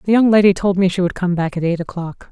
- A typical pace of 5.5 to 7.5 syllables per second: Yes, 6.5 syllables/s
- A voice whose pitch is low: No, medium, 185 Hz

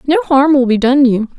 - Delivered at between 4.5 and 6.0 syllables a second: Yes, 5.2 syllables/s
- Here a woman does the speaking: Yes, female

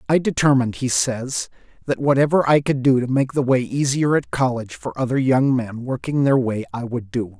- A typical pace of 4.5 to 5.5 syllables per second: Yes, 5.3 syllables/s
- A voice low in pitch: Yes, low, 130 Hz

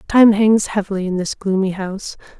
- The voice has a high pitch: Yes, high, 200 Hz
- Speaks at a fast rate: No, average, 175 wpm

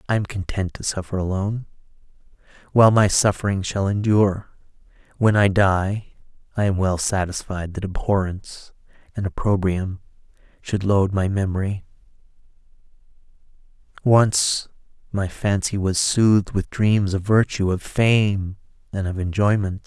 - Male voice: Yes, male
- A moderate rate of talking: No, slow, 120 wpm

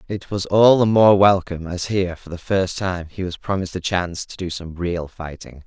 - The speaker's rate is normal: No, fast, 235 wpm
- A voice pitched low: Yes, very low, 90 Hz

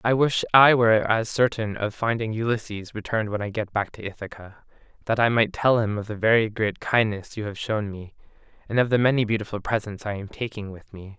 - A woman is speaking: No, male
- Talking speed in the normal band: No, fast, 220 wpm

